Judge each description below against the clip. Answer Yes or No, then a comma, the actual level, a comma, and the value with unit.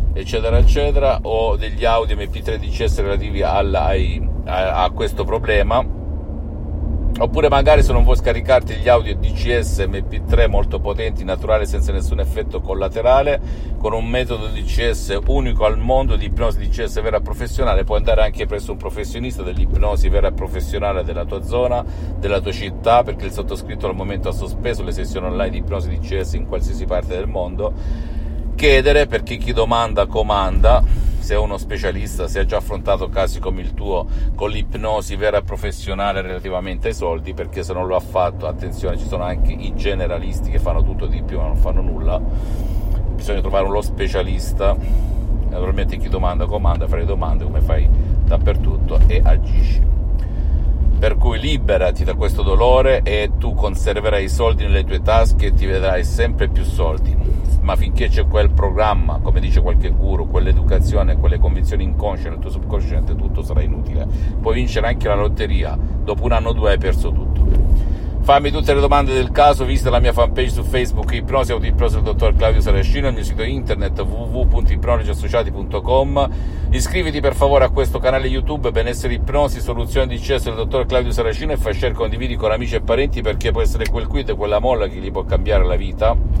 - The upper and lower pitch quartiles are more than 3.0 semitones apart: Yes, average, 5.2 semitones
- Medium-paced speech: No, fast, 175 wpm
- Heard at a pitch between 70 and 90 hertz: Yes, very low, 80 Hz